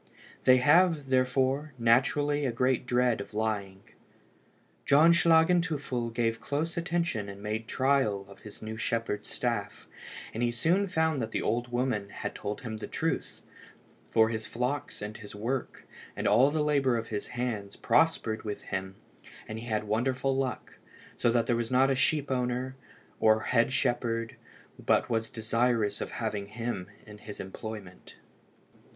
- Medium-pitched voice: No, low, 120 Hz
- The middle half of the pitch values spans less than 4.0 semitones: Yes, average, 3.6 semitones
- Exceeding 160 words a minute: No, average, 155 wpm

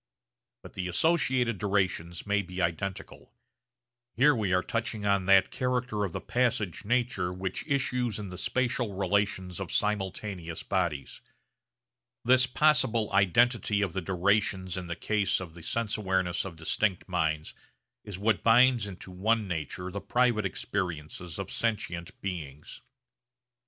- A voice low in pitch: Yes, low, 100 Hz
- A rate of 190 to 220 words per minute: No, average, 140 wpm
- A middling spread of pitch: Yes, average, 4.0 semitones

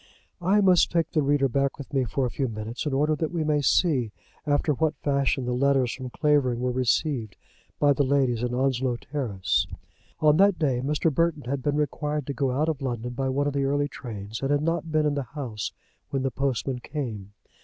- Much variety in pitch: No, average, 3.0 semitones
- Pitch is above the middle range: No, medium, 140 Hz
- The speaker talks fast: Yes, fast, 215 wpm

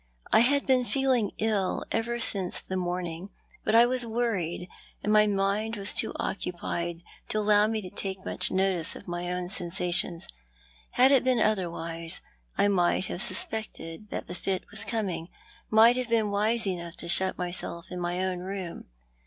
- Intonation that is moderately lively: Yes, average, 3.8 semitones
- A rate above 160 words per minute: Yes, average, 175 wpm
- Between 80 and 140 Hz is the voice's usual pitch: No, high, 195 Hz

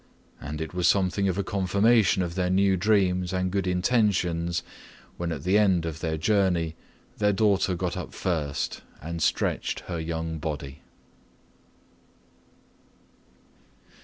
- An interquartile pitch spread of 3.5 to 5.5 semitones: No, average, 2.9 semitones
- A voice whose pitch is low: Yes, very low, 90 Hz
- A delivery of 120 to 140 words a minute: Yes, slow, 135 wpm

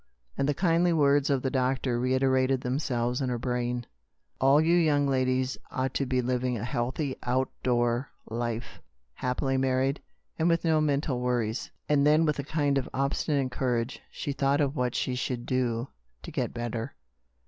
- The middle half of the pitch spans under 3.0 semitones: Yes, narrow, 2.4 semitones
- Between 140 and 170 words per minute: No, average, 180 wpm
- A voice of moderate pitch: No, low, 130 Hz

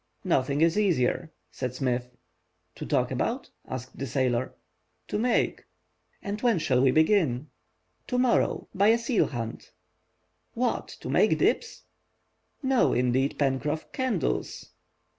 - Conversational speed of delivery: No, slow, 125 wpm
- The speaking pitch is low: No, medium, 150 Hz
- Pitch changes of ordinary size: No, wide, 8.7 semitones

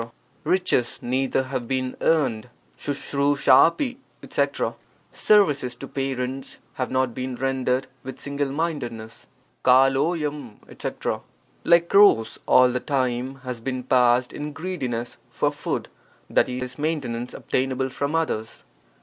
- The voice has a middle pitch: No, low, 130 Hz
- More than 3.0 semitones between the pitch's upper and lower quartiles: No, narrow, 2.5 semitones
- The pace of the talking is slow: Yes, slow, 125 wpm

